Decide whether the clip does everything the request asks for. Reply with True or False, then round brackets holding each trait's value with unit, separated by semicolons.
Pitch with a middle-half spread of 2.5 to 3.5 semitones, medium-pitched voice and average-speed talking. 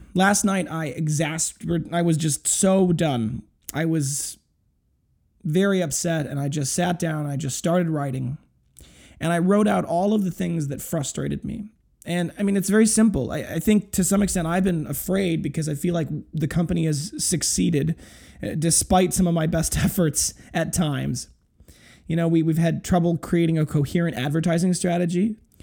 True (2.8 semitones; 165 Hz; 180 wpm)